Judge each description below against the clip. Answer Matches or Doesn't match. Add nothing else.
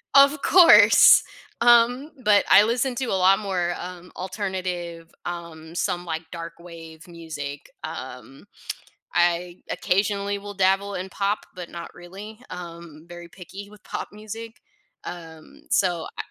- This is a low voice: Doesn't match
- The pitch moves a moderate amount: Matches